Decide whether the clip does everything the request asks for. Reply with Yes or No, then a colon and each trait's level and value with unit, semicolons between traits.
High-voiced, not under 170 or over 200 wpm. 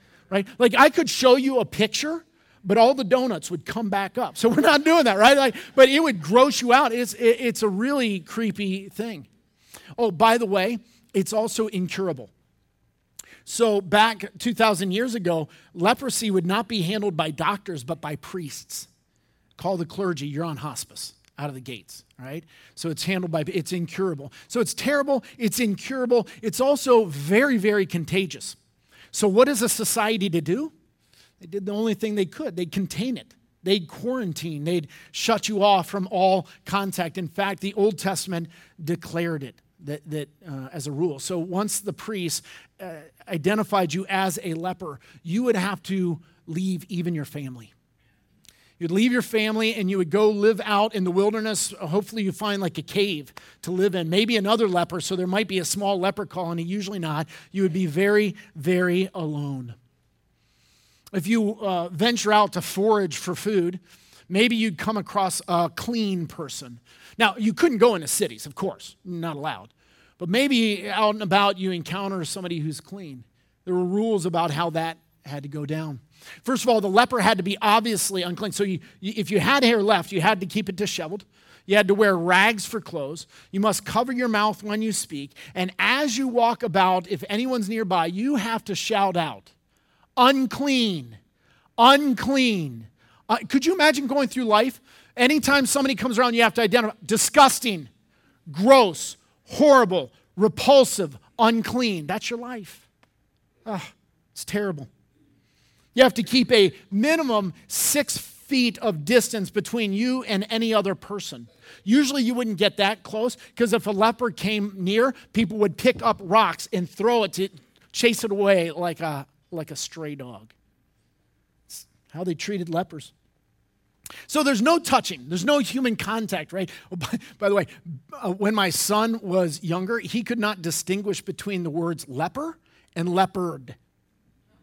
Yes: high, 200 Hz; average, 175 wpm